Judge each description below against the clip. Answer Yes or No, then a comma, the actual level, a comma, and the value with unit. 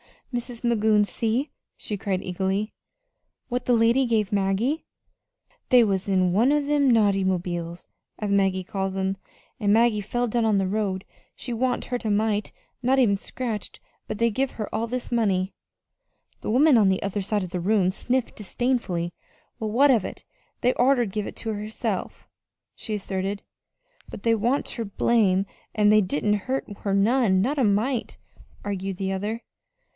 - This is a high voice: Yes, high, 210 Hz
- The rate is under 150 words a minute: No, average, 170 wpm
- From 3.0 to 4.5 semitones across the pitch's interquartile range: Yes, average, 3.7 semitones